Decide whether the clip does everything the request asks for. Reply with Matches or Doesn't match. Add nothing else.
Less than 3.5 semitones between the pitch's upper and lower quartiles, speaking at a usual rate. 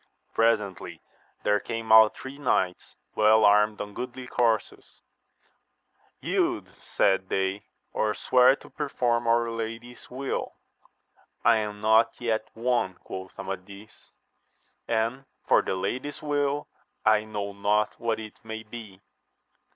Doesn't match